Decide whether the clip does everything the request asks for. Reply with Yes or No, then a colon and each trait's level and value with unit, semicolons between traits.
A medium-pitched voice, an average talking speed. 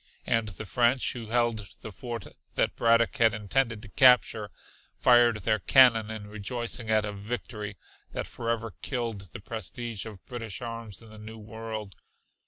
No: low, 110 Hz; average, 160 wpm